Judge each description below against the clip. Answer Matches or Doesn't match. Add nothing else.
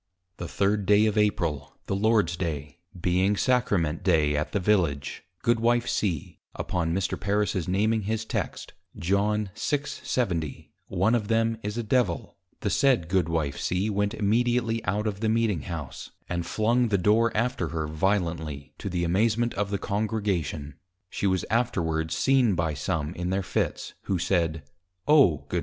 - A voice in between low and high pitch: Doesn't match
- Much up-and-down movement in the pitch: Doesn't match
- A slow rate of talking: Doesn't match